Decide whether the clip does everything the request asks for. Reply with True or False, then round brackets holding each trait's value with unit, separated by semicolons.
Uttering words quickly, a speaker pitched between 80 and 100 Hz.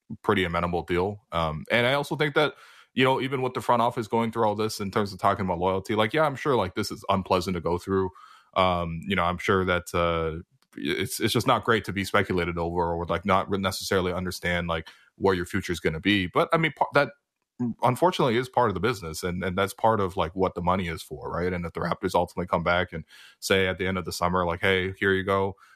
True (255 wpm; 95 Hz)